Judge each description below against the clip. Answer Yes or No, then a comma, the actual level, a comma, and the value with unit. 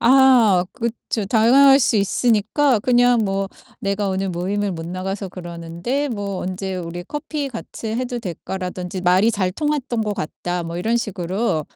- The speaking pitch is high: Yes, high, 200 Hz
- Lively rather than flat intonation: No, average, 4.8 semitones